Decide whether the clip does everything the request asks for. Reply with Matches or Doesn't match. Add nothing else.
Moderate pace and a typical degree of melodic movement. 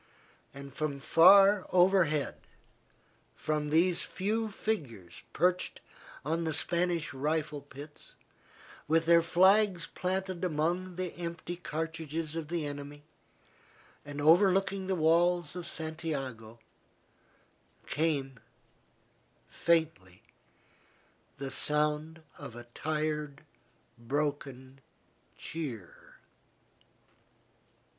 Doesn't match